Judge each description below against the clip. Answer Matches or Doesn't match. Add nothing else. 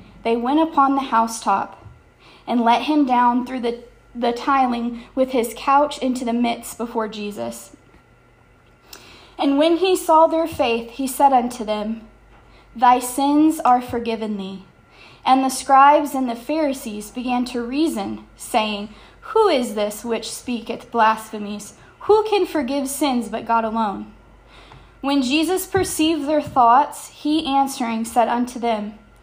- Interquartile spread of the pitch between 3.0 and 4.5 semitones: Matches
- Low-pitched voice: Doesn't match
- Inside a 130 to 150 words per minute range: Matches